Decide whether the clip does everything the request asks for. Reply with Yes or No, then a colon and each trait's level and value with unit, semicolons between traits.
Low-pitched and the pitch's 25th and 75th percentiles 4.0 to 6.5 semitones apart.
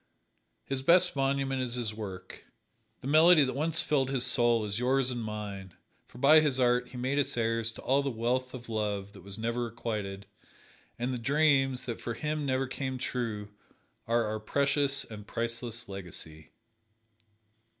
No: low, 125 Hz; average, 3.6 semitones